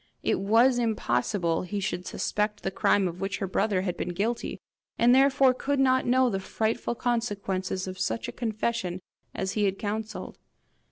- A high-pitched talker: Yes, high, 210 Hz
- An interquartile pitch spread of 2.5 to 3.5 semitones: No, average, 4.0 semitones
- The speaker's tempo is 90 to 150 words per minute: No, average, 170 wpm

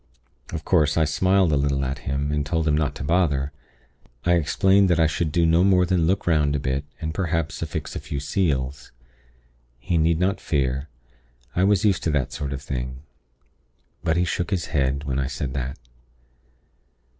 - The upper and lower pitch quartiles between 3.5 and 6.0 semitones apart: Yes, average, 3.8 semitones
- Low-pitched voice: Yes, very low, 75 Hz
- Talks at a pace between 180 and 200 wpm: Yes, average, 190 wpm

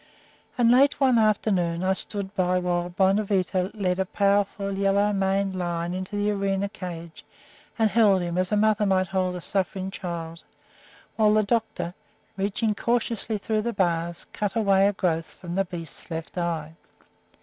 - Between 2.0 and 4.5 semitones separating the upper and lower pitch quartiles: Yes, narrow, 2.6 semitones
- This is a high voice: Yes, high, 195 Hz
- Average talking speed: Yes, average, 160 wpm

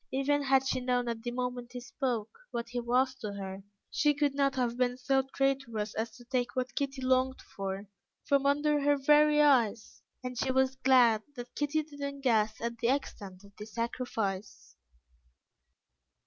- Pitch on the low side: No, very high, 255 Hz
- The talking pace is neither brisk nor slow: Yes, average, 175 wpm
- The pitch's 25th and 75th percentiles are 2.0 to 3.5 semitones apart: Yes, average, 2.8 semitones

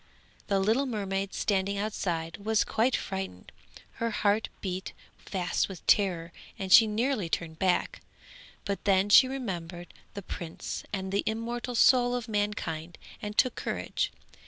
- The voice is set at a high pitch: Yes, high, 200 Hz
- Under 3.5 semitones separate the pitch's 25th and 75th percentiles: Yes, average, 3.0 semitones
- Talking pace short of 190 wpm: Yes, average, 140 wpm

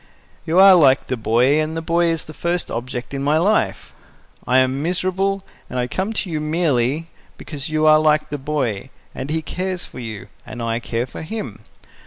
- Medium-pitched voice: Yes, medium, 155 Hz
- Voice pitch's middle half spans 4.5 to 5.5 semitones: Yes, average, 5.0 semitones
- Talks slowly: No, average, 200 wpm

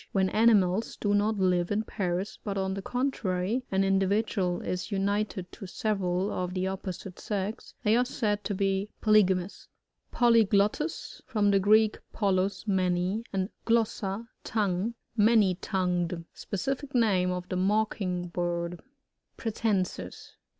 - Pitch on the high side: Yes, high, 195 Hz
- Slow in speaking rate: Yes, slow, 130 wpm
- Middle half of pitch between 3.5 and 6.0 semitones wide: No, average, 2.8 semitones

